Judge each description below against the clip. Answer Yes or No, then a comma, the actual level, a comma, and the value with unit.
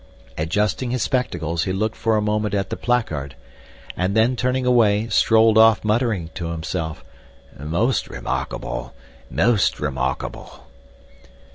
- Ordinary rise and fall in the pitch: No, wide, 5.7 semitones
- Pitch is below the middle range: Yes, low, 105 Hz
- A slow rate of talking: Yes, slow, 120 wpm